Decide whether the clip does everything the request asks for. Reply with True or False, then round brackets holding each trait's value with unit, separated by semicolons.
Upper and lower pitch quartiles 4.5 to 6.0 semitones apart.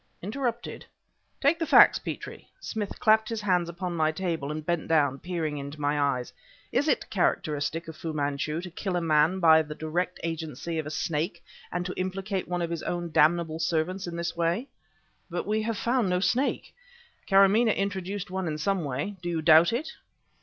False (3.7 semitones)